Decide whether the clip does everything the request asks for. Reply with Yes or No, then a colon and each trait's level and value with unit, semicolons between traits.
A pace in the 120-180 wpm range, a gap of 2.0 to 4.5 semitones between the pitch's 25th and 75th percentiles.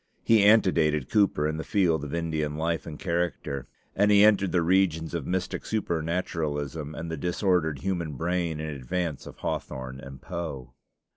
Yes: average, 160 wpm; average, 3.3 semitones